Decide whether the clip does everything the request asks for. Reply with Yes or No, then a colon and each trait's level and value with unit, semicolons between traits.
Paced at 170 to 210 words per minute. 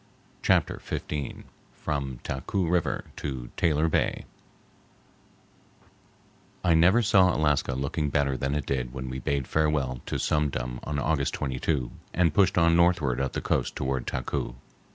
No: average, 145 wpm